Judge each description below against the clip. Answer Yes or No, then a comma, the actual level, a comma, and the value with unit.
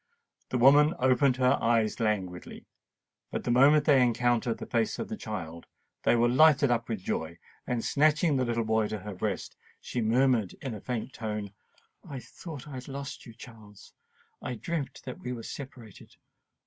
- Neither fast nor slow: Yes, average, 170 wpm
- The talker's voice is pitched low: Yes, low, 120 Hz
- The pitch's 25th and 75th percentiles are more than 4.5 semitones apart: No, average, 3.6 semitones